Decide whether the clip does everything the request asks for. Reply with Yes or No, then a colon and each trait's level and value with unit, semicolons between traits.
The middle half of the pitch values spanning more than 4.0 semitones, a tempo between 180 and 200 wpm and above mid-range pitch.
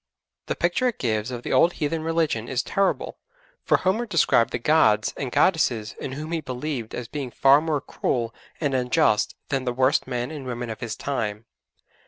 No: average, 4.8 semitones; average, 190 wpm; low, 130 Hz